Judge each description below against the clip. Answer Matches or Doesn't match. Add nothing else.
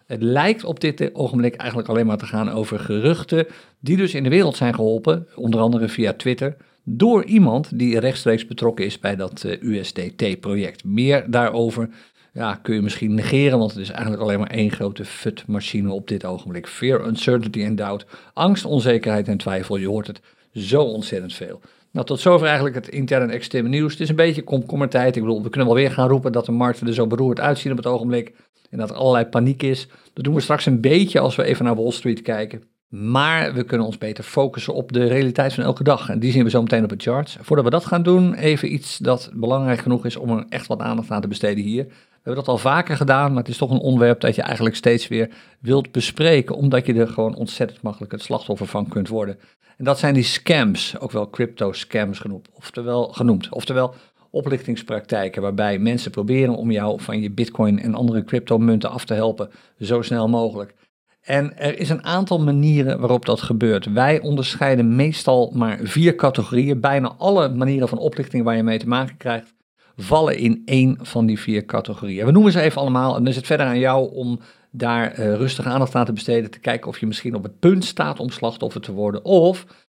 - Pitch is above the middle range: Doesn't match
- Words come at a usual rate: Doesn't match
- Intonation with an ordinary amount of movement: Matches